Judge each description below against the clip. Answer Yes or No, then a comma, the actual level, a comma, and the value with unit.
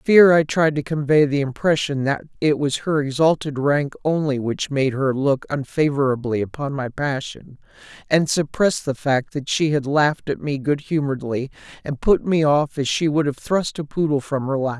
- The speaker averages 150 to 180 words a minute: No, average, 200 wpm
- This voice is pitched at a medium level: Yes, medium, 145 Hz